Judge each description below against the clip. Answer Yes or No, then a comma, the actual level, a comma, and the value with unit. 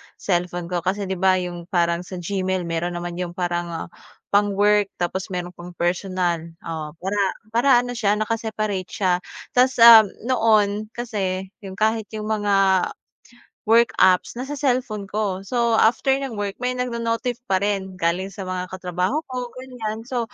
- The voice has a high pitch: Yes, high, 195 Hz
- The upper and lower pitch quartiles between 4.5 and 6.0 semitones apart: No, average, 3.8 semitones